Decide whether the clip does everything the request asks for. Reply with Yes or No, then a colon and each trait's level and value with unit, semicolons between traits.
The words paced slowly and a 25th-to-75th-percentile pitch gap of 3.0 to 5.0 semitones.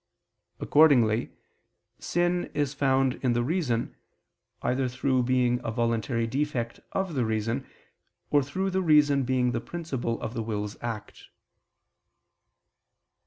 Yes: slow, 120 wpm; average, 3.8 semitones